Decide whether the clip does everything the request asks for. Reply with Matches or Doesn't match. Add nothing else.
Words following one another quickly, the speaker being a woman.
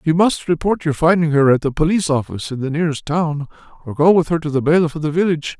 Doesn't match